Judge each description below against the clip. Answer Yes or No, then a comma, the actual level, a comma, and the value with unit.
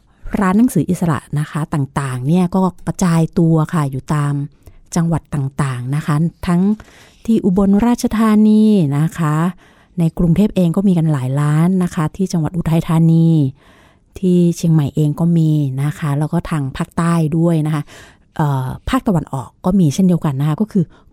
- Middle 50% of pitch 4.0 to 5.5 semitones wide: No, average, 3.5 semitones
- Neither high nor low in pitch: Yes, medium, 165 Hz